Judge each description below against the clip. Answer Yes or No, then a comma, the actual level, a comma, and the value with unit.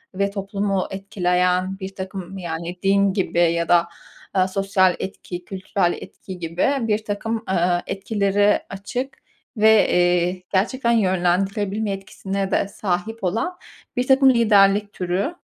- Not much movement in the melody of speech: Yes, narrow, 2.3 semitones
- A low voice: No, high, 195 Hz